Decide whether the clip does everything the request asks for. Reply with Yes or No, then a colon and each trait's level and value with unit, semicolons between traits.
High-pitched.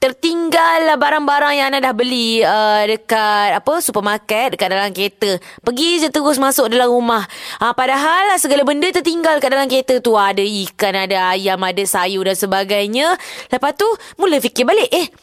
Yes: very high, 250 Hz